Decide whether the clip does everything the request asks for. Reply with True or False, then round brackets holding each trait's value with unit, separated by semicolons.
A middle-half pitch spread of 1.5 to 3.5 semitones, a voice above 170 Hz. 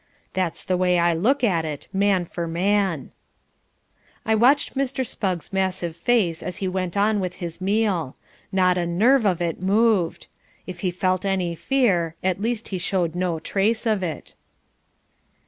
True (3.2 semitones; 185 Hz)